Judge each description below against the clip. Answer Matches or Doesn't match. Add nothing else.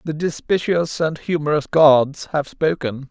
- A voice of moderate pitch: Matches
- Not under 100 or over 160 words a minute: Matches